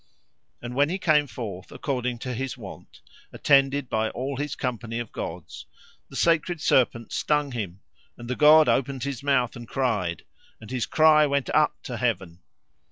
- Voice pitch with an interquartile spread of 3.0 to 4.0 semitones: Yes, average, 3.6 semitones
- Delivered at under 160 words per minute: No, average, 165 wpm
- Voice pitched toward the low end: Yes, low, 130 Hz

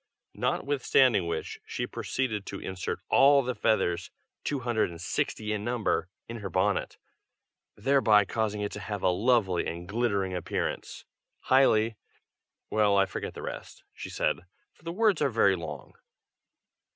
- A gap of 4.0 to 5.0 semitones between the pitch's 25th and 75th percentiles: Yes, average, 4.4 semitones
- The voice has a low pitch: Yes, low, 105 Hz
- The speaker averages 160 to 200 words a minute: No, average, 150 wpm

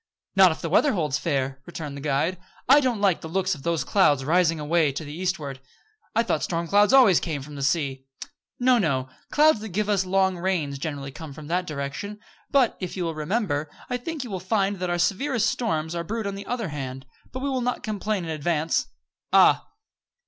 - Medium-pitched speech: Yes, medium, 175 Hz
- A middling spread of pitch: No, wide, 5.7 semitones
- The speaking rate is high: Yes, fast, 215 wpm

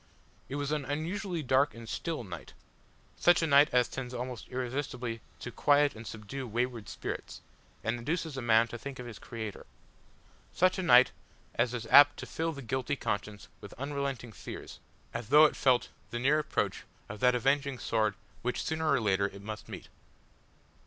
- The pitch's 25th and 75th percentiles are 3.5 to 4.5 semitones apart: Yes, average, 3.8 semitones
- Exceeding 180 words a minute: No, average, 175 wpm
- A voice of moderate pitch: No, low, 125 Hz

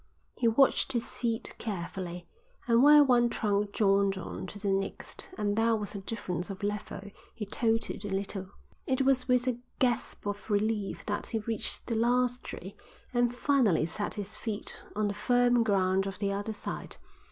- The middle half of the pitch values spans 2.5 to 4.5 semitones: Yes, average, 3.3 semitones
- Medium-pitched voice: No, high, 210 Hz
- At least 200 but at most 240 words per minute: No, average, 175 wpm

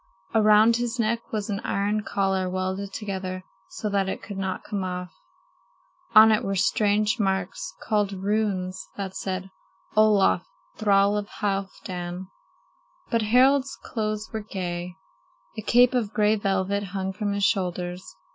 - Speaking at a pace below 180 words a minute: Yes, average, 140 wpm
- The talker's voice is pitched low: No, high, 200 Hz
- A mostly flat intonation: Yes, narrow, 2.2 semitones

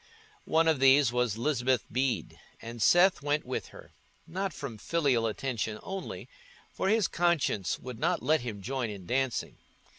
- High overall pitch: No, low, 135 Hz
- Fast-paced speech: No, average, 150 wpm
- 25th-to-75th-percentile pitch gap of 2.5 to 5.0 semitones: No, wide, 5.5 semitones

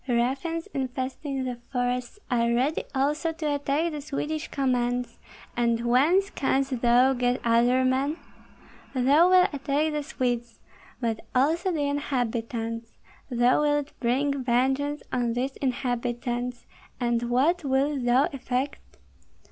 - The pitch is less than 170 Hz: No, very high, 260 Hz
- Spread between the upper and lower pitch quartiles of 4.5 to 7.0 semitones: No, average, 3.0 semitones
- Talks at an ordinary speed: No, slow, 125 wpm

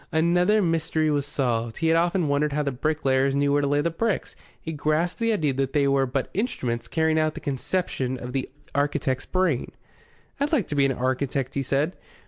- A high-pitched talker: No, medium, 145 Hz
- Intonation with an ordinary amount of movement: Yes, average, 3.4 semitones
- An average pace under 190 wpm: No, fast, 205 wpm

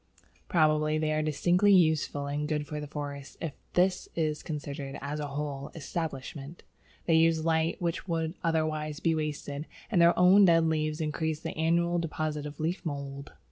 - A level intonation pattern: Yes, narrow, 2.0 semitones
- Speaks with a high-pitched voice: No, medium, 155 Hz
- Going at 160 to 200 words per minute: Yes, average, 170 wpm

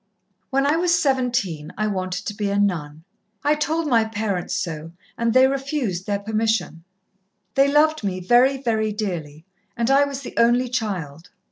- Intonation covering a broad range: Yes, wide, 6.5 semitones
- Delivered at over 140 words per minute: Yes, average, 165 wpm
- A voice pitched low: No, high, 220 Hz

